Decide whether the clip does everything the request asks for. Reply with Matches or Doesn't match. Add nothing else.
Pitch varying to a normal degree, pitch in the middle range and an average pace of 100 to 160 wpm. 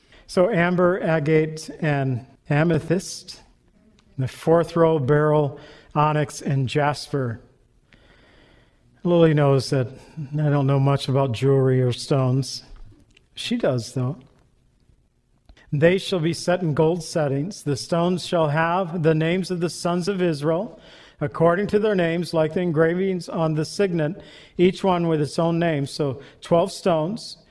Matches